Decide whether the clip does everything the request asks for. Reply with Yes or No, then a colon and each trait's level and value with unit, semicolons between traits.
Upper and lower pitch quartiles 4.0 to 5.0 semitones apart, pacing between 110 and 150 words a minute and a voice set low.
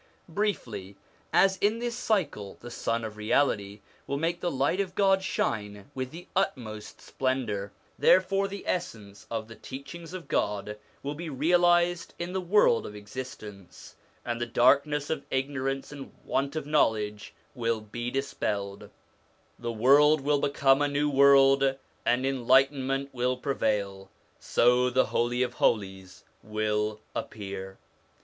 No: wide, 5.6 semitones; average, 140 wpm; low, 130 Hz